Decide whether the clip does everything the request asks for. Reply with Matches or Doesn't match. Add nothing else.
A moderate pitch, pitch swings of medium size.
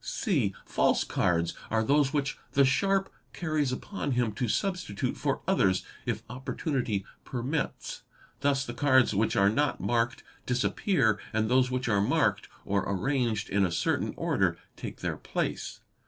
Doesn't match